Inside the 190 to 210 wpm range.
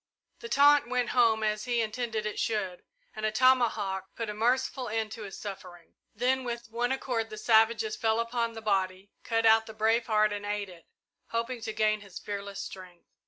Yes: average, 195 wpm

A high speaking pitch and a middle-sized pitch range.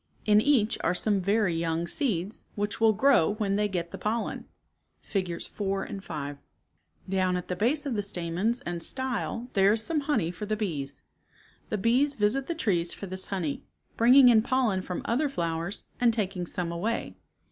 Yes: high, 205 Hz; average, 4.6 semitones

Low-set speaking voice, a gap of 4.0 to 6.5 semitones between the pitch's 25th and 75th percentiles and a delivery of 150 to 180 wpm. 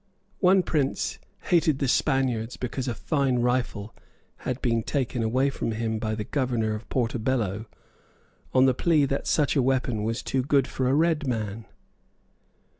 No: low, 125 Hz; average, 3.4 semitones; average, 160 wpm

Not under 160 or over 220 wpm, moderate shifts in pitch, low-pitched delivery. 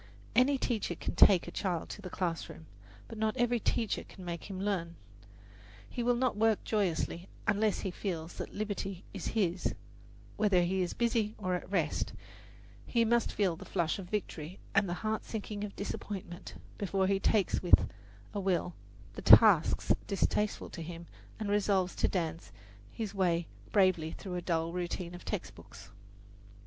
No: average, 165 wpm; average, 3.3 semitones; high, 195 Hz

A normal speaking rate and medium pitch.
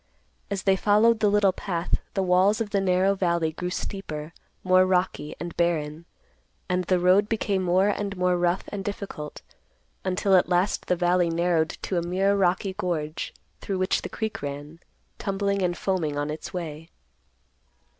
Yes: average, 165 wpm; medium, 180 Hz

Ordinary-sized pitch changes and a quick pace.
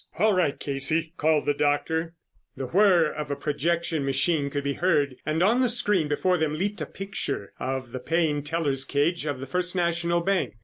No: average, 3.5 semitones; average, 190 wpm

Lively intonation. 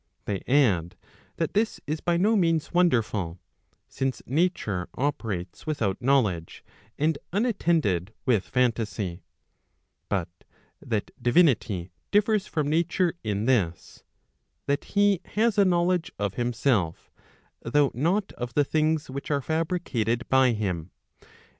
Yes: wide, 8.4 semitones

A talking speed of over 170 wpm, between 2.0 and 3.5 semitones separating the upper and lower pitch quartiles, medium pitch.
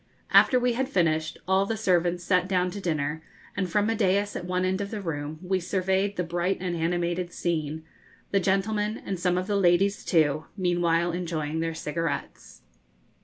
Yes: average, 180 wpm; average, 2.8 semitones; medium, 180 Hz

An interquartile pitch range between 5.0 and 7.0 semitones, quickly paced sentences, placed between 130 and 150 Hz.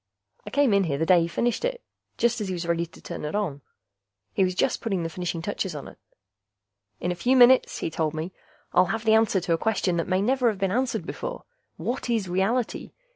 No: average, 5.3 semitones; fast, 235 wpm; high, 190 Hz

